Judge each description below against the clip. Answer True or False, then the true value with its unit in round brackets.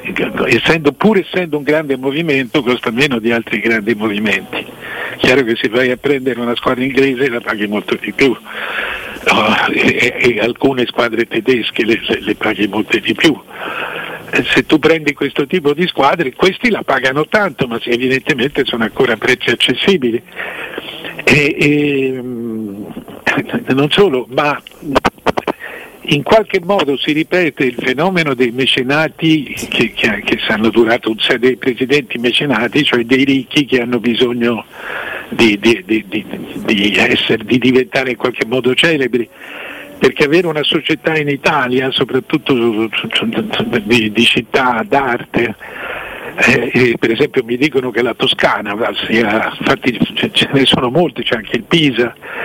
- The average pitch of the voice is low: True (130 Hz)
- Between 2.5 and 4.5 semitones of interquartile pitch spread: True (4.0 semitones)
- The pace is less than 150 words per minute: False (155 wpm)